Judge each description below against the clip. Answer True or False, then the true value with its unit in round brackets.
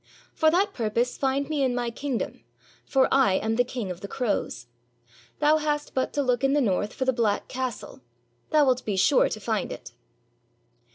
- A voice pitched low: False (250 Hz)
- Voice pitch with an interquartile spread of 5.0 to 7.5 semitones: False (4.2 semitones)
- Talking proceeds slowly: False (195 wpm)